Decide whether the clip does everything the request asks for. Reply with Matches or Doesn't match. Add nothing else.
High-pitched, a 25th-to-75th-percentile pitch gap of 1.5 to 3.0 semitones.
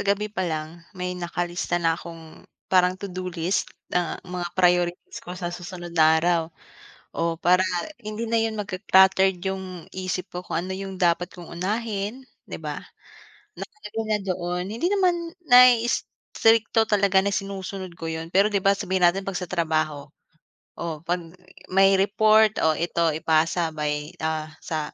Doesn't match